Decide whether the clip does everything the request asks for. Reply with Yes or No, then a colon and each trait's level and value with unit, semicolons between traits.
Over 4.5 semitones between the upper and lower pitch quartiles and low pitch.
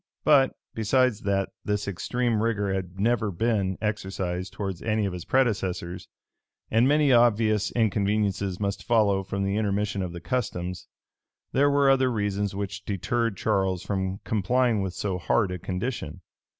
No: average, 3.3 semitones; low, 100 Hz